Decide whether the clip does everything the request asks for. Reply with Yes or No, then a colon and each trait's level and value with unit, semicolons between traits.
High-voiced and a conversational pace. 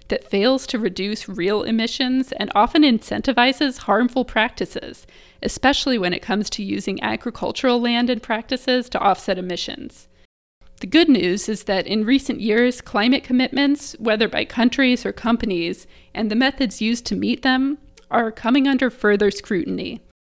Yes: high, 235 Hz; average, 150 wpm